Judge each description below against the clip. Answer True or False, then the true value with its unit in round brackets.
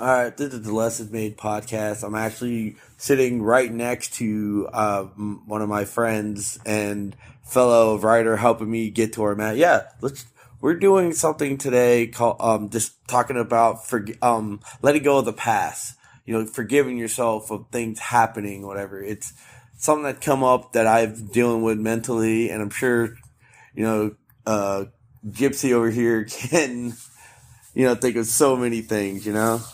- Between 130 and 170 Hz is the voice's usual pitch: False (115 Hz)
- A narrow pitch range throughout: True (2.3 semitones)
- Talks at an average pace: True (170 wpm)